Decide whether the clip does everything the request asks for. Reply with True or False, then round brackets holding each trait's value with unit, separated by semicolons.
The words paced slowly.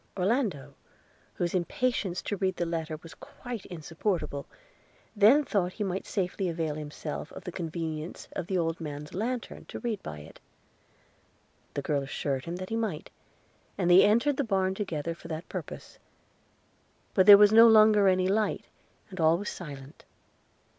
False (160 wpm)